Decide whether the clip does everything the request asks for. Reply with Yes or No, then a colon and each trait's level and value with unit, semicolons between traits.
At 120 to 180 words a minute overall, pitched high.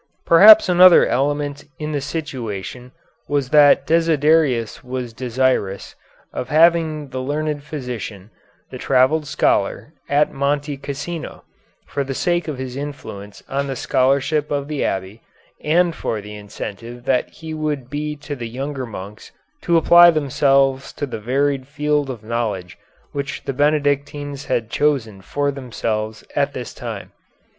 No: average, 140 wpm; medium, 140 Hz